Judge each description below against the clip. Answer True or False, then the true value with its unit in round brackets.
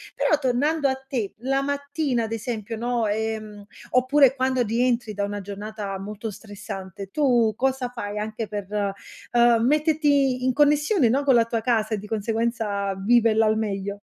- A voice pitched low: False (230 Hz)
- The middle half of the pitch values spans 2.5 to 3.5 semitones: False (3.9 semitones)